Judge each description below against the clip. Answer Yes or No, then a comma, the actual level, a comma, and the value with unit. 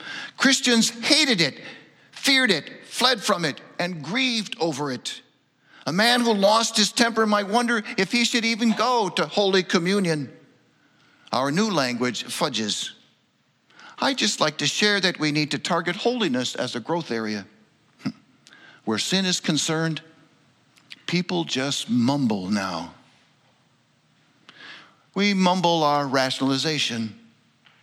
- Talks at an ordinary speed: No, slow, 125 wpm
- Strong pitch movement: Yes, wide, 8.0 semitones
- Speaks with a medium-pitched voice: Yes, medium, 175 Hz